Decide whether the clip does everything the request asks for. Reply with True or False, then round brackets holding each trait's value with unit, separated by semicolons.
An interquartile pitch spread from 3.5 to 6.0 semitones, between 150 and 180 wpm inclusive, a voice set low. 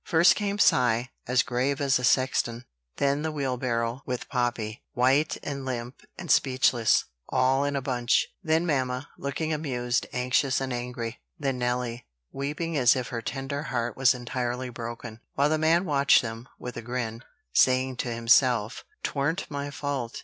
False (2.6 semitones; 160 wpm; 130 Hz)